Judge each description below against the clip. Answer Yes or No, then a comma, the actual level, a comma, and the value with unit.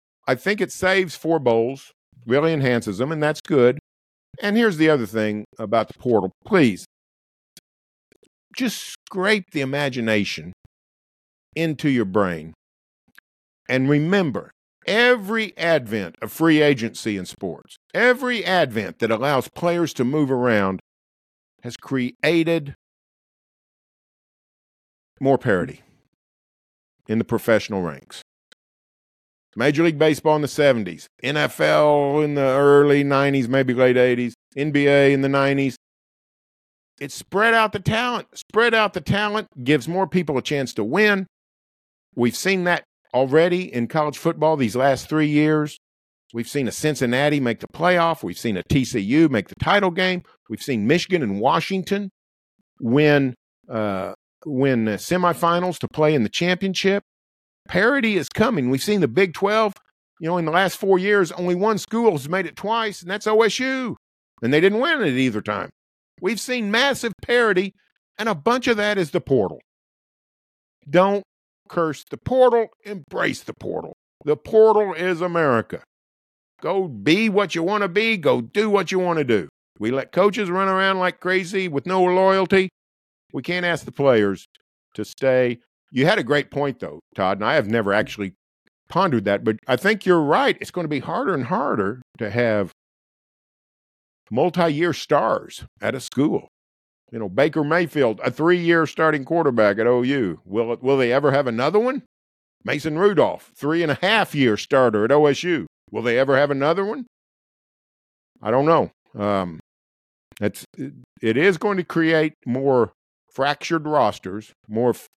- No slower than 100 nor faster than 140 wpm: No, average, 155 wpm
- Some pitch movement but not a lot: No, wide, 7.5 semitones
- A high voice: No, medium, 155 Hz